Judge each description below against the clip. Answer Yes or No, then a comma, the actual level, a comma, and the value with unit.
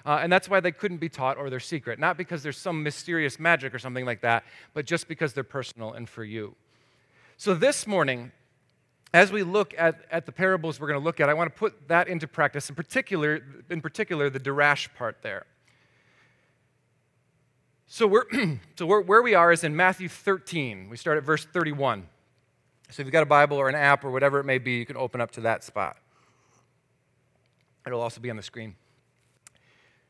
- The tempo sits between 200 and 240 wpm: Yes, fast, 205 wpm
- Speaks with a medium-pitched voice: Yes, medium, 145 Hz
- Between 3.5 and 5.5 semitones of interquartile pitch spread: Yes, average, 4.6 semitones